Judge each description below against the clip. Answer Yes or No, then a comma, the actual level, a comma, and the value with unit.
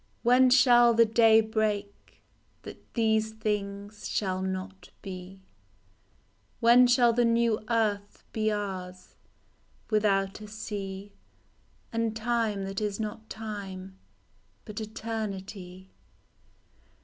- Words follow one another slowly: Yes, slow, 100 wpm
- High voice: Yes, high, 215 Hz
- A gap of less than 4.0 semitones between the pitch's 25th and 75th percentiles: Yes, narrow, 2.6 semitones